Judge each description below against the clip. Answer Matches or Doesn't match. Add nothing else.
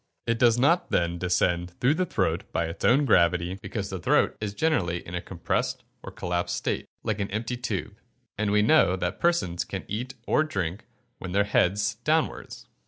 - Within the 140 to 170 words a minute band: Doesn't match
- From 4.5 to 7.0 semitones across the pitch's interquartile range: Matches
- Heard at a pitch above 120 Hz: Doesn't match